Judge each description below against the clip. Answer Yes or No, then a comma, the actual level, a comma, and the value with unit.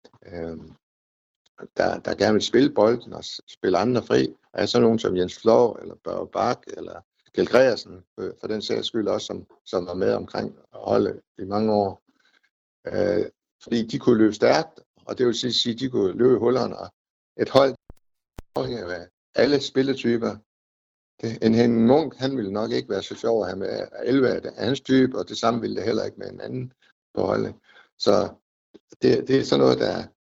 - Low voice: Yes, low, 115 Hz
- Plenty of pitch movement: Yes, wide, 6.0 semitones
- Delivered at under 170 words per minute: No, average, 195 wpm